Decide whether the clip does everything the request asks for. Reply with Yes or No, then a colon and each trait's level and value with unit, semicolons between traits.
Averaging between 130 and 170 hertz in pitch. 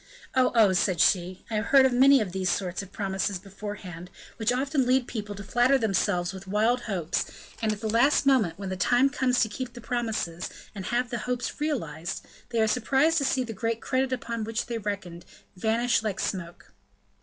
No: high, 220 Hz